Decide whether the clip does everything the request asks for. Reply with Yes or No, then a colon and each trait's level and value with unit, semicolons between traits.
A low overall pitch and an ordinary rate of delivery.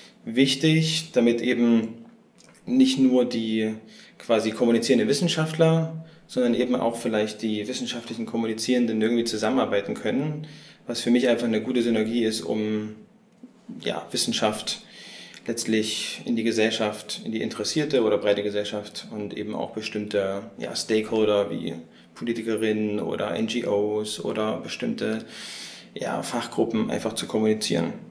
No: low, 115 Hz; slow, 120 wpm